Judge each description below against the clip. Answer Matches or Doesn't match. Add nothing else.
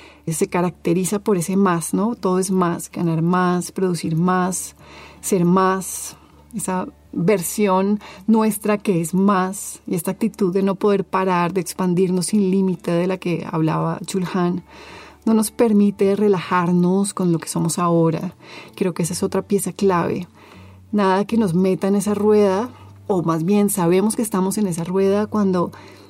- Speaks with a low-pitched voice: Doesn't match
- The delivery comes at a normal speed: Matches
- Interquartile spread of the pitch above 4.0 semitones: Doesn't match